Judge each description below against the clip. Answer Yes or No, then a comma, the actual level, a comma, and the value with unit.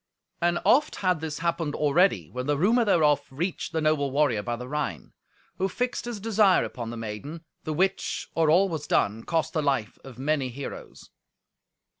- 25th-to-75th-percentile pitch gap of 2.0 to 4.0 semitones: No, average, 4.9 semitones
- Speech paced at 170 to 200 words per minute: Yes, average, 180 wpm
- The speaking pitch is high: No, medium, 155 Hz